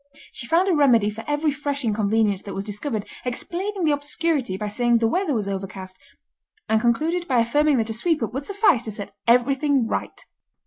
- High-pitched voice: Yes, high, 245 Hz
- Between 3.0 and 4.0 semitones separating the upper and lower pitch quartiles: No, wide, 5.6 semitones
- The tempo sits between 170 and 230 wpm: Yes, average, 190 wpm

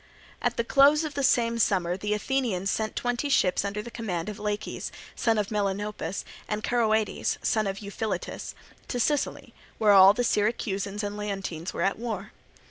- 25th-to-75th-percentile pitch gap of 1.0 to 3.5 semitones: Yes, average, 2.8 semitones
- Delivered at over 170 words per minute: No, average, 165 wpm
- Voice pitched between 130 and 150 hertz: No, high, 210 Hz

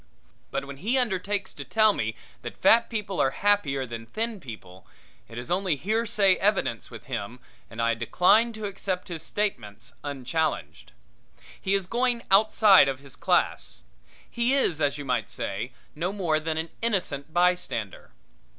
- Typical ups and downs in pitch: No, wide, 7.6 semitones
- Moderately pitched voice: Yes, medium, 175 Hz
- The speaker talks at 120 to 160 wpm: Yes, average, 155 wpm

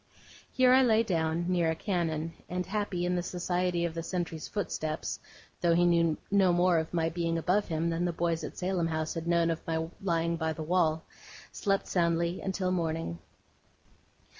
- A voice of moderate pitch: Yes, medium, 170 Hz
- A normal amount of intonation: No, narrow, 1.9 semitones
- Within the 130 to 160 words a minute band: No, average, 185 wpm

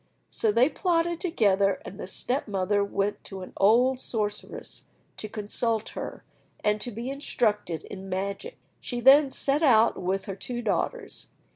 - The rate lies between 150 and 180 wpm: Yes, average, 155 wpm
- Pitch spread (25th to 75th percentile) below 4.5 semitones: No, average, 4.9 semitones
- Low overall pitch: No, high, 220 Hz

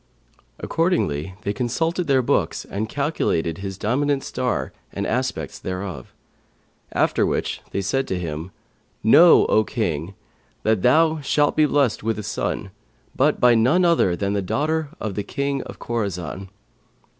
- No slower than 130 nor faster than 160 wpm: Yes, average, 150 wpm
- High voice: No, low, 110 Hz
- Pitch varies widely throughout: Yes, wide, 7.0 semitones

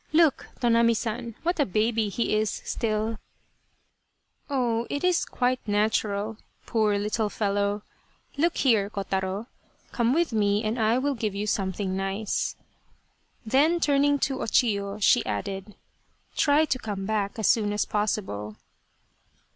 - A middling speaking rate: Yes, average, 145 wpm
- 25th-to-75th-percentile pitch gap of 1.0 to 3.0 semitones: No, average, 3.4 semitones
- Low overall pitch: No, high, 215 Hz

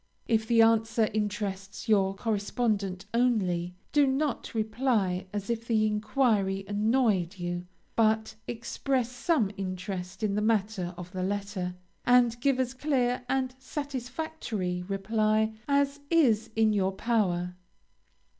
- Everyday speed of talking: No, slow, 125 wpm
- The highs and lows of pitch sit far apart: No, average, 4.0 semitones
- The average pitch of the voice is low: No, high, 220 Hz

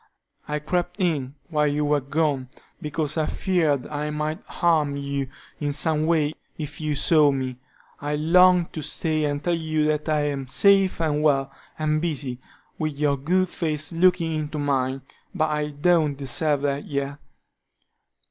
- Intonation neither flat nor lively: No, narrow, 2.0 semitones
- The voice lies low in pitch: No, medium, 150 Hz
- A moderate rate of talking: Yes, average, 160 wpm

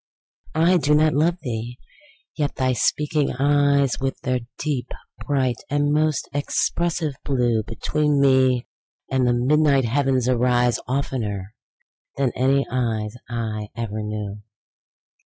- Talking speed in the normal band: No, slow, 120 wpm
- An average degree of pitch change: Yes, average, 3.3 semitones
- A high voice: No, low, 130 Hz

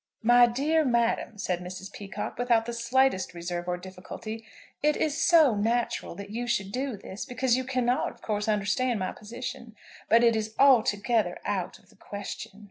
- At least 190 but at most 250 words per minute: No, average, 175 wpm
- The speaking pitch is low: No, high, 225 Hz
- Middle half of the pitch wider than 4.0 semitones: No, average, 3.7 semitones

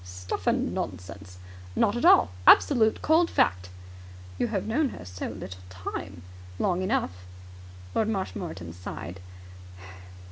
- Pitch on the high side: No, very low, 95 Hz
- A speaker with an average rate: No, slow, 120 wpm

